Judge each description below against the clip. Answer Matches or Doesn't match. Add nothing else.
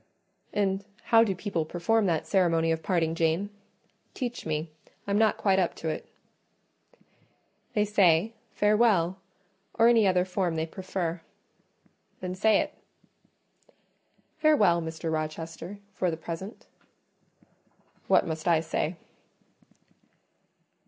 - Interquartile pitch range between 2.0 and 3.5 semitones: Doesn't match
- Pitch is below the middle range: Doesn't match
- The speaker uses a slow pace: Matches